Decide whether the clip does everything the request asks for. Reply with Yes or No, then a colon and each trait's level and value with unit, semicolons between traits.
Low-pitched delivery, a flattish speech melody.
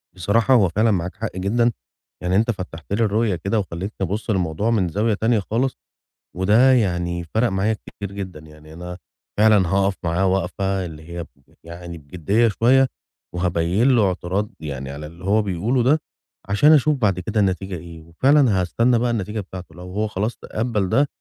No: very low, 95 Hz; average, 4.1 semitones